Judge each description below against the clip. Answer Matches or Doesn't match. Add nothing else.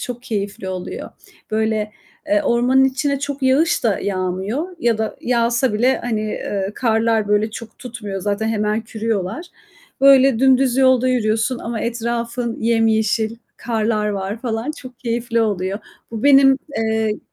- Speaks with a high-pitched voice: Matches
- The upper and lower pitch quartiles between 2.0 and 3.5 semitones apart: Matches